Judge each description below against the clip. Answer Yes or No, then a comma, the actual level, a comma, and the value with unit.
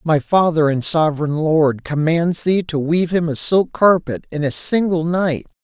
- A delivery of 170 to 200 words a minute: Yes, average, 180 wpm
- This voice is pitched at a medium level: Yes, medium, 160 Hz